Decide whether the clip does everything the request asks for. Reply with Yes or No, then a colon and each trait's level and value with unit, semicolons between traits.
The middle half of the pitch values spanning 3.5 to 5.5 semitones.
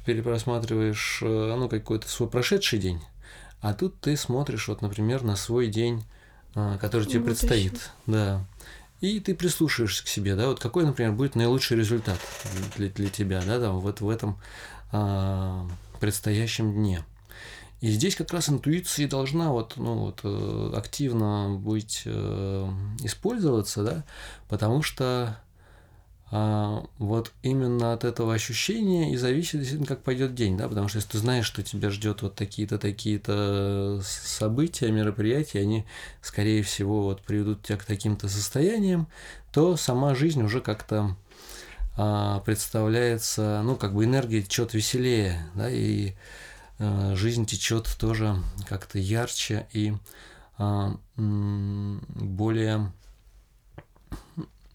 No: average, 3.0 semitones